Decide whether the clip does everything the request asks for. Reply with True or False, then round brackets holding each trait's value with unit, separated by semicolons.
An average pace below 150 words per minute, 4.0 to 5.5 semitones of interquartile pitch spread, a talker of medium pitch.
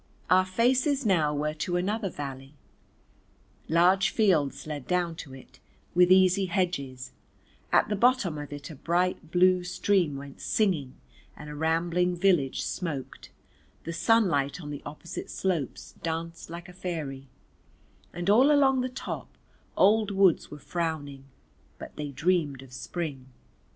True (140 wpm; 4.3 semitones; 170 Hz)